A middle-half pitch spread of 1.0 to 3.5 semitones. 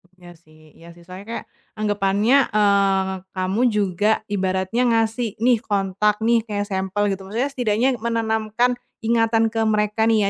Yes: average, 2.8 semitones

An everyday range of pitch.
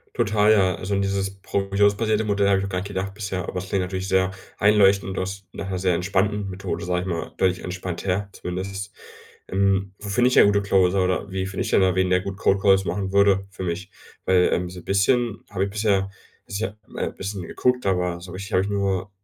No: narrow, 1.3 semitones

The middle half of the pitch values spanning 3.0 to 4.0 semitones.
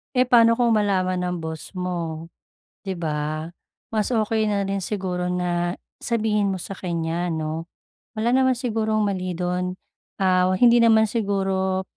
Yes: average, 3.5 semitones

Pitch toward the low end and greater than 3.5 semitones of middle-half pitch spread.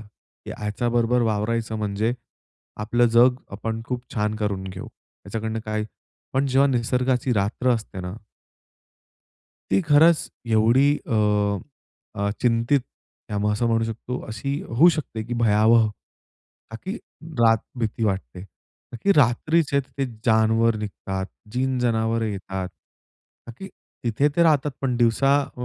No: low, 115 Hz; average, 2.9 semitones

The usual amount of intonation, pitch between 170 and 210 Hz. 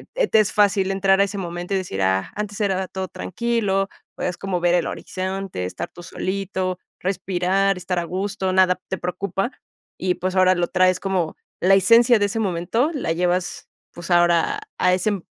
No: narrow, 1.8 semitones; high, 190 Hz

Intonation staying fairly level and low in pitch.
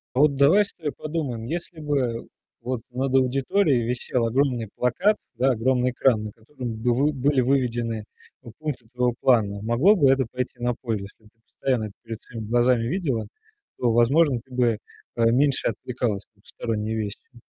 No: average, 3.0 semitones; low, 125 Hz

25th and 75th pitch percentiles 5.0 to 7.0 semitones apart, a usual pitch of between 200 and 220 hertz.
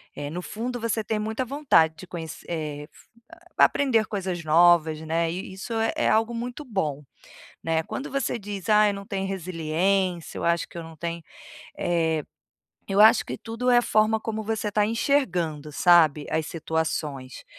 No: average, 5.3 semitones; medium, 185 Hz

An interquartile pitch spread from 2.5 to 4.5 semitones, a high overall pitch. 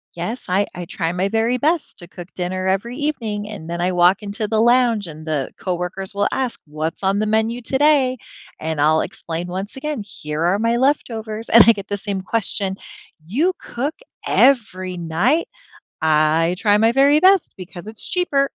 No: average, 5.3 semitones; high, 205 Hz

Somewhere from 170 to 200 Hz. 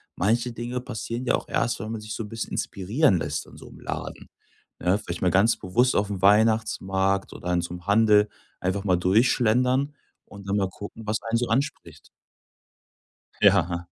No: low, 105 Hz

